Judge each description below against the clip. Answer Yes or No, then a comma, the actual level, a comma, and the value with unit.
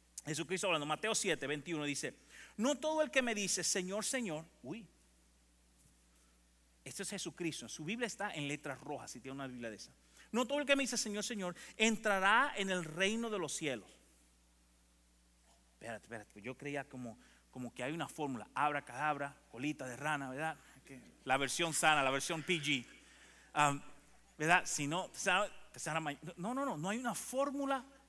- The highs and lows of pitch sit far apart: Yes, wide, 7.7 semitones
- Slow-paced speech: No, average, 165 wpm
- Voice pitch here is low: No, medium, 150 Hz